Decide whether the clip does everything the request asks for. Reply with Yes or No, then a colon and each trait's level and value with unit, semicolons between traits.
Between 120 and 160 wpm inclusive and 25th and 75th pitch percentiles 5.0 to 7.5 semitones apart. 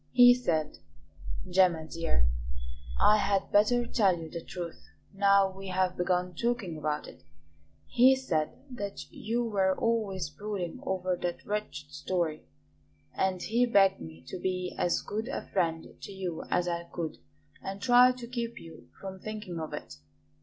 No: average, 155 wpm; average, 4.0 semitones